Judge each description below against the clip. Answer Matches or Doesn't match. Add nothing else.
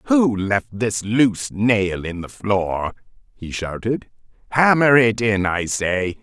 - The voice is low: Matches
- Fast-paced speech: Doesn't match